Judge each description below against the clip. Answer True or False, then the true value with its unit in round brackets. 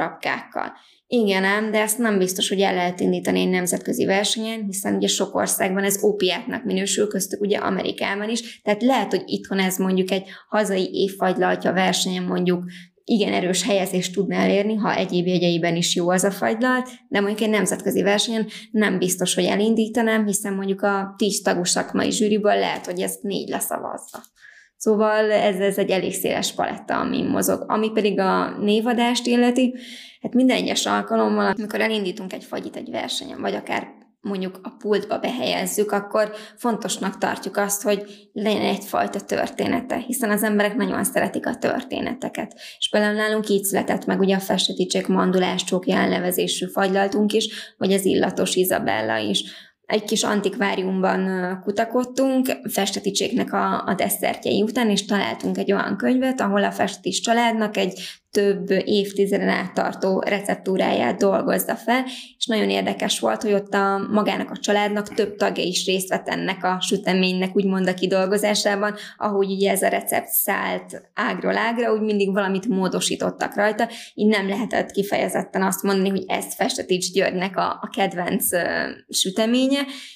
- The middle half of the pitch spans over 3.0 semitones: False (2.4 semitones)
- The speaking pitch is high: True (200 Hz)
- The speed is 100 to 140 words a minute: False (155 wpm)